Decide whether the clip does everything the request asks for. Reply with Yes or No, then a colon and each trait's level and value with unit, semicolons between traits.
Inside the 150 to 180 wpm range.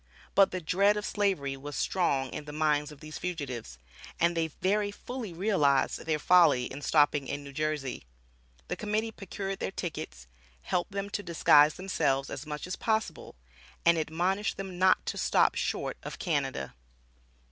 Yes: average, 165 wpm